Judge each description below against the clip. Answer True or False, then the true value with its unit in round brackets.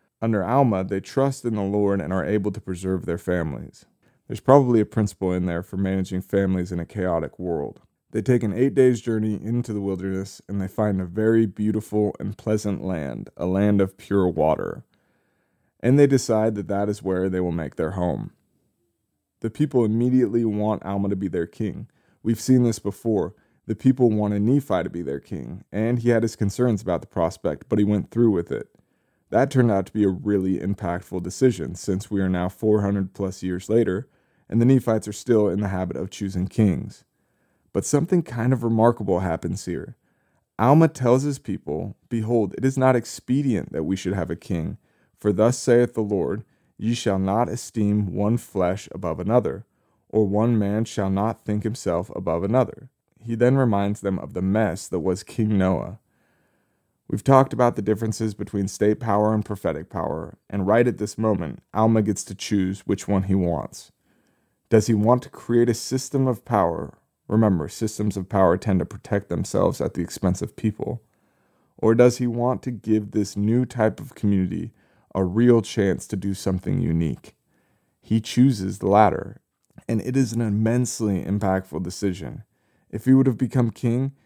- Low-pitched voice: True (105 Hz)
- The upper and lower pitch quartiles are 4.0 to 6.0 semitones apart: False (3.6 semitones)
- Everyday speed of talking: True (185 wpm)